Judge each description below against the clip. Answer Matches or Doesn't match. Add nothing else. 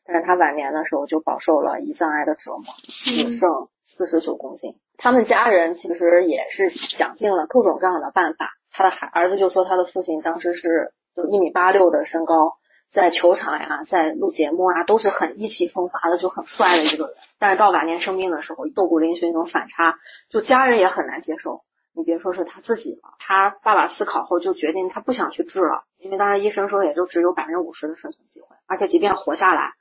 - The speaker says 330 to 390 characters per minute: Matches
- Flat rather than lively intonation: Doesn't match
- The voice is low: Doesn't match